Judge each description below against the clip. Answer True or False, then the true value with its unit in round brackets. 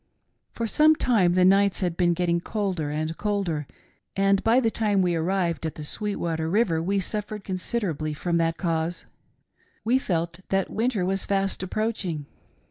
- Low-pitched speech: False (185 Hz)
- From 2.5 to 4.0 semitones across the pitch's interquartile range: True (3.7 semitones)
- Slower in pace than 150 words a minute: False (160 wpm)